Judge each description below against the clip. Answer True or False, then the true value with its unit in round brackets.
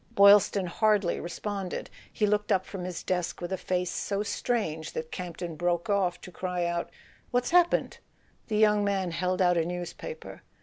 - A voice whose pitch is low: False (185 Hz)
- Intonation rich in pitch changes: False (2.9 semitones)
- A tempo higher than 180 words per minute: False (170 wpm)